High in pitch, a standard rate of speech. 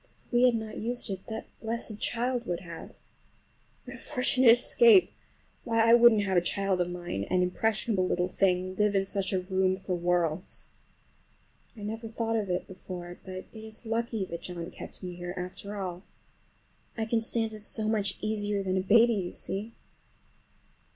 Yes: high, 200 Hz; average, 180 wpm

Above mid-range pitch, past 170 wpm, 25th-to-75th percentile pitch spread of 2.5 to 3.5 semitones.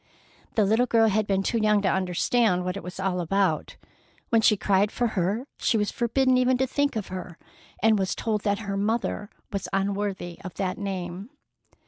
Yes: high, 200 Hz; average, 190 wpm; average, 2.8 semitones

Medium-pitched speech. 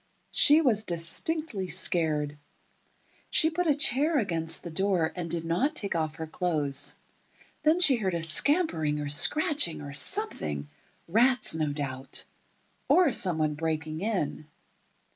Yes: medium, 170 Hz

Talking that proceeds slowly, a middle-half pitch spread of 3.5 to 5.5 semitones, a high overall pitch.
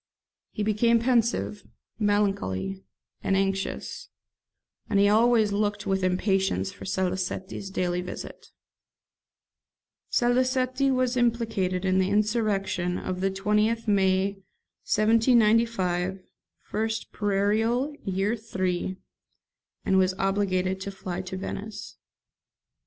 No: slow, 100 wpm; average, 2.9 semitones; high, 200 Hz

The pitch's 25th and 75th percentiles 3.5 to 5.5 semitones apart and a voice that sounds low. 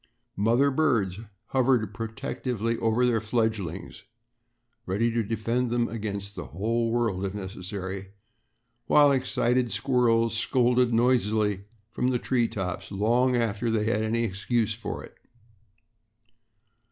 No: average, 2.9 semitones; low, 115 Hz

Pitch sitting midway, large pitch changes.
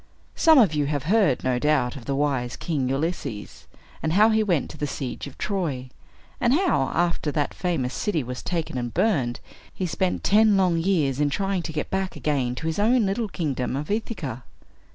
Yes: medium, 155 Hz; wide, 6.4 semitones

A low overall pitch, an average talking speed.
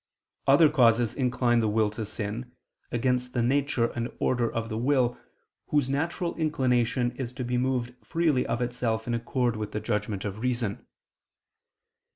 Yes: low, 120 Hz; average, 160 wpm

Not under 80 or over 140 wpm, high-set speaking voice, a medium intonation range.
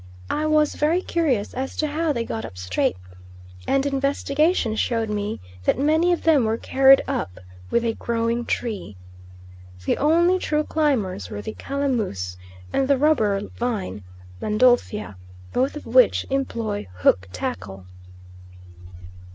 No: slow, 135 wpm; high, 245 Hz; wide, 6.4 semitones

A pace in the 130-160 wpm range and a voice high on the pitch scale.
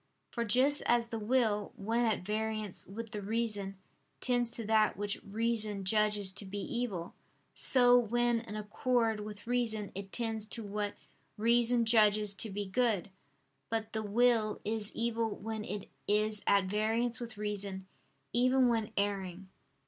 Yes: average, 150 wpm; high, 215 Hz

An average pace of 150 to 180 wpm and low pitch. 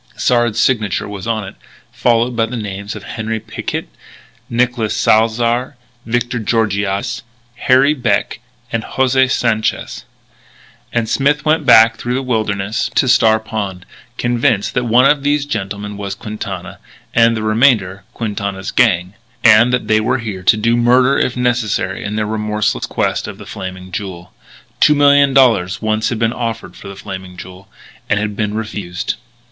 Yes: average, 155 wpm; low, 110 Hz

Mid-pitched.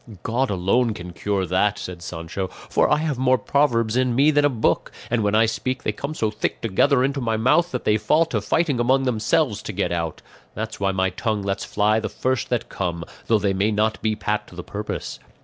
No: low, 110 Hz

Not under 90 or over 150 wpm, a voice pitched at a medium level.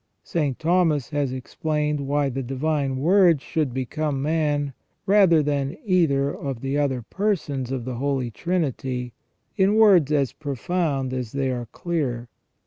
Yes: average, 140 wpm; medium, 145 Hz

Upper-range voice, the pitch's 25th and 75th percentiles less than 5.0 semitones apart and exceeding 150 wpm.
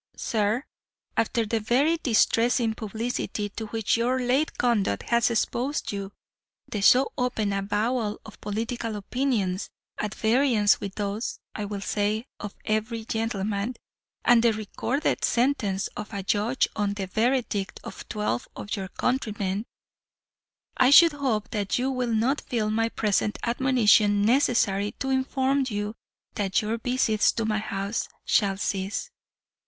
No: high, 220 Hz; average, 3.1 semitones; average, 140 wpm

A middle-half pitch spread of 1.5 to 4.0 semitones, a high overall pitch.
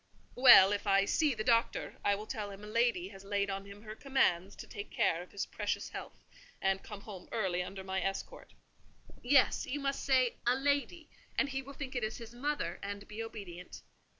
No: average, 4.6 semitones; high, 210 Hz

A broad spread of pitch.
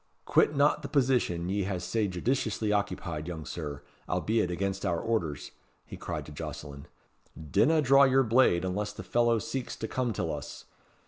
Yes: wide, 6.4 semitones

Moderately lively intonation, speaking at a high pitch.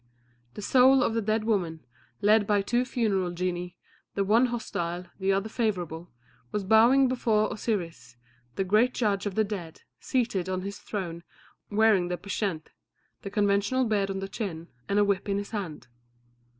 Yes: average, 3.2 semitones; high, 200 Hz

